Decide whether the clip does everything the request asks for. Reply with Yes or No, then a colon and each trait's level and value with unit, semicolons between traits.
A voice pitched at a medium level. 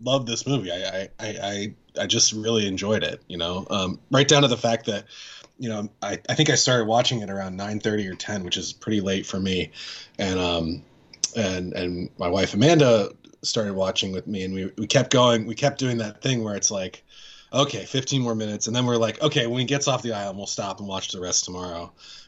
No: low, 110 Hz